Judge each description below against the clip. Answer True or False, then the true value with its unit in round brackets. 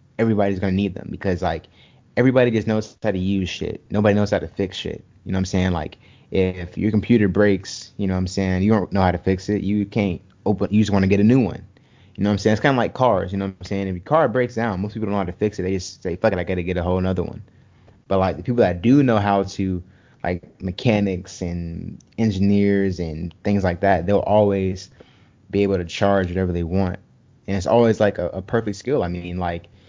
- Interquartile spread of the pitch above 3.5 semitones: False (2.4 semitones)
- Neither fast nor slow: False (260 wpm)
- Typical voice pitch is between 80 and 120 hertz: True (100 Hz)